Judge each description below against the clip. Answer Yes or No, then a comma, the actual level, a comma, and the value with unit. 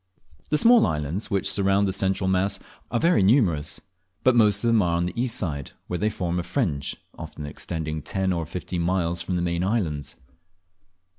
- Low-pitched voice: Yes, very low, 95 Hz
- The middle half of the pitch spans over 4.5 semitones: No, average, 3.4 semitones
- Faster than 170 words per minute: Yes, average, 190 wpm